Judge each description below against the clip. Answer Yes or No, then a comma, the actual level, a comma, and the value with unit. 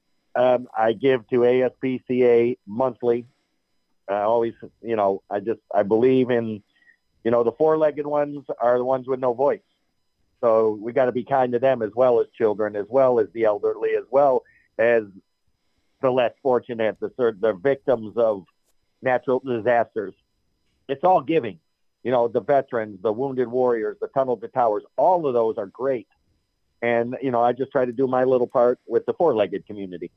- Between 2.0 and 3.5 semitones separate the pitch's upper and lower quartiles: Yes, average, 2.8 semitones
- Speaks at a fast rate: No, average, 180 wpm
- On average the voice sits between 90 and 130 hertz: Yes, low, 125 Hz